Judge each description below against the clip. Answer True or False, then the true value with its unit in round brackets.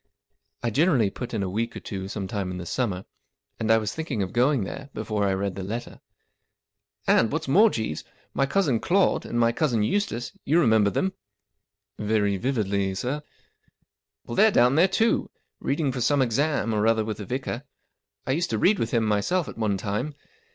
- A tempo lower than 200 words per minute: False (205 wpm)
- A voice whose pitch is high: False (115 Hz)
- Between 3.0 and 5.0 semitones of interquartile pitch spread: False (5.5 semitones)